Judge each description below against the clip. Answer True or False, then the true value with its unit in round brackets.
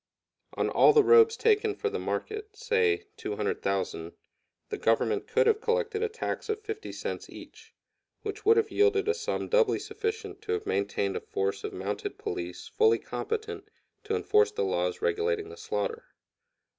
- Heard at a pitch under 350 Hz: False (435 Hz)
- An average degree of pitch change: False (1.2 semitones)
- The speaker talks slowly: False (165 wpm)